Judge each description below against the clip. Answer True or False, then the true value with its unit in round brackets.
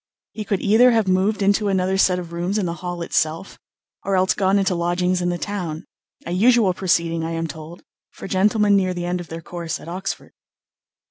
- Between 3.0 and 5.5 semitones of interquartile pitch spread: False (2.6 semitones)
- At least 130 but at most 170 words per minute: False (205 wpm)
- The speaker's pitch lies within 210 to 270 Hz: False (185 Hz)